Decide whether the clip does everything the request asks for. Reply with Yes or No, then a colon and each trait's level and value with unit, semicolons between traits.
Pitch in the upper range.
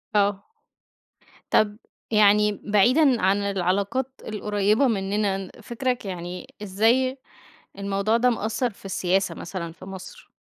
Yes: high, 205 Hz